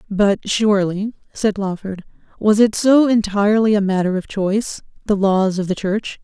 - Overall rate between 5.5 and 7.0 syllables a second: No, 4.8 syllables/s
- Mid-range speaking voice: No, high, 205 Hz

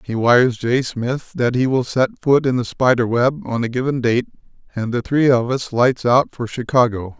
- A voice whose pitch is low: Yes, low, 125 Hz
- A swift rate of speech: Yes, fast, 215 wpm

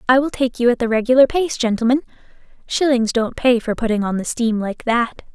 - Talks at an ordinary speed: No, fast, 215 wpm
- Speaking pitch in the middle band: No, high, 240 Hz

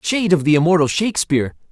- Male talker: Yes, male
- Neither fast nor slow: Yes, average, 175 wpm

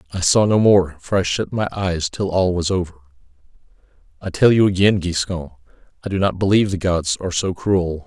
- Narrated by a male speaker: Yes, male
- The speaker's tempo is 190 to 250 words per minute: Yes, average, 200 wpm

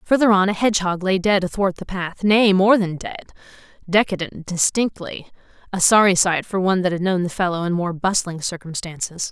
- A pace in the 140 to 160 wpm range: No, average, 180 wpm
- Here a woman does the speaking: Yes, female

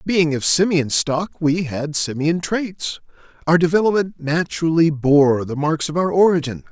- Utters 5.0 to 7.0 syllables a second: No, 4.5 syllables/s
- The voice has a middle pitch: Yes, medium, 160 Hz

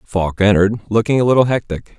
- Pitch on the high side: No, low, 105 Hz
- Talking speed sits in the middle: Yes, average, 180 wpm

